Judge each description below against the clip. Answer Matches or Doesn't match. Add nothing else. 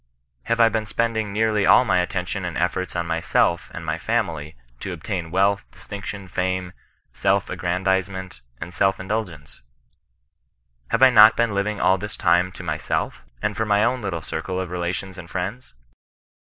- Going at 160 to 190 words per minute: Matches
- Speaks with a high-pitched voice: Doesn't match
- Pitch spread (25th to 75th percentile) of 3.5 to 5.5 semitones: Doesn't match